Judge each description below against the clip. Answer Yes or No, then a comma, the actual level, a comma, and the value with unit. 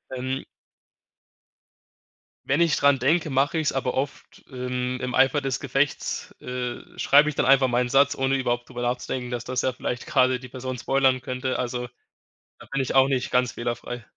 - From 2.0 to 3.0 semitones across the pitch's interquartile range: No, narrow, 1.5 semitones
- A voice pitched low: Yes, low, 130 Hz